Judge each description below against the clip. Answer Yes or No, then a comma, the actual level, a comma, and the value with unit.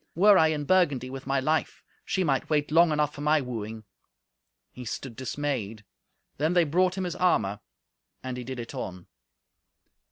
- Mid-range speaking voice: Yes, medium, 145 Hz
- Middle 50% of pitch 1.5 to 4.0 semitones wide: No, average, 4.4 semitones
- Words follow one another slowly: No, average, 170 wpm